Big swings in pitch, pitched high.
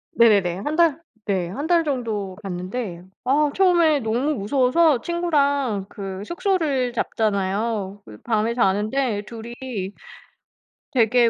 Yes: wide, 6.1 semitones; high, 235 Hz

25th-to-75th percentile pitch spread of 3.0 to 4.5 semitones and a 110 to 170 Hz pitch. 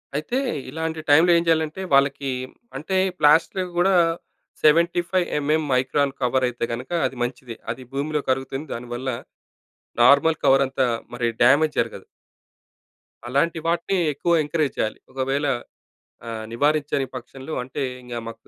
Yes: average, 3.6 semitones; medium, 140 Hz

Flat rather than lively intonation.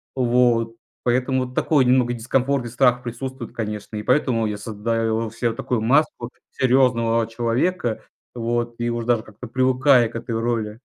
Yes: narrow, 1.9 semitones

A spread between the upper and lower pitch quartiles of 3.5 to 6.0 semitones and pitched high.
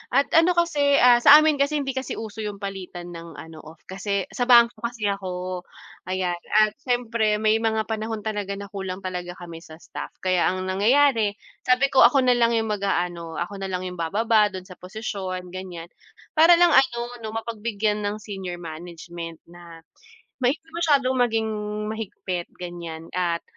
Yes: average, 4.6 semitones; high, 205 Hz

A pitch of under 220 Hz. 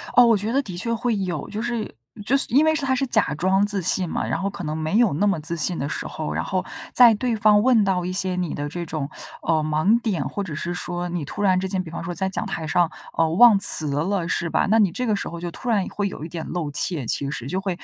Yes: medium, 185 Hz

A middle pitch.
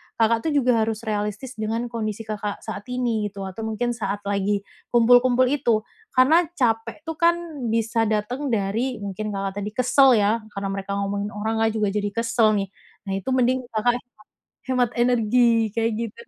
No: high, 225 Hz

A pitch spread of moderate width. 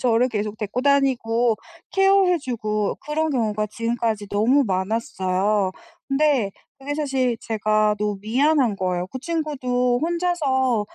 Yes: average, 4.9 semitones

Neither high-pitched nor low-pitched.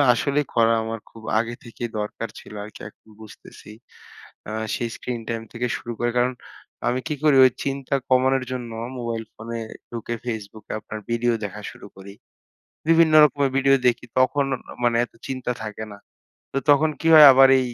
No: low, 120 Hz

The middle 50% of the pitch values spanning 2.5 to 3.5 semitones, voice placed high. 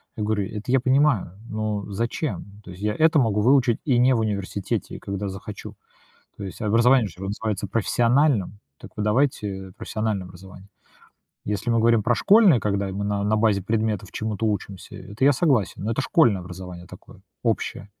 No: average, 3.0 semitones; low, 105 Hz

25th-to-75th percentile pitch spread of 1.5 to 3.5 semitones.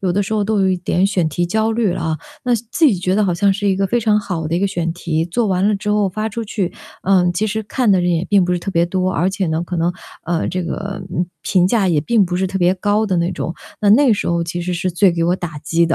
Yes: average, 2.9 semitones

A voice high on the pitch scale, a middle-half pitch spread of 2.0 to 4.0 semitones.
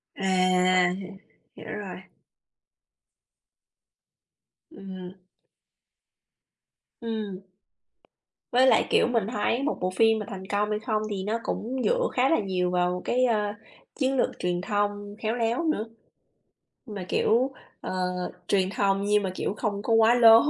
Yes: high, 210 Hz; average, 3.4 semitones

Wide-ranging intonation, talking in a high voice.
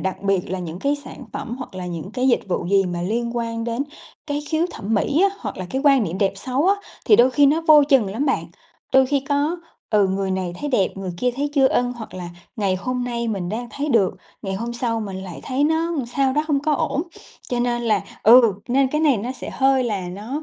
Yes: wide, 5.9 semitones; high, 240 Hz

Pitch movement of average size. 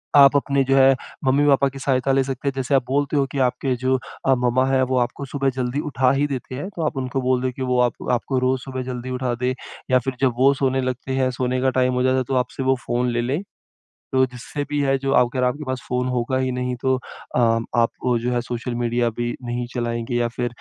No: narrow, 1.4 semitones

